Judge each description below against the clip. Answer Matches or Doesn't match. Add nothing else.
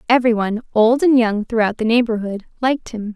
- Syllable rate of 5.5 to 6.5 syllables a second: Matches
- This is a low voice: Doesn't match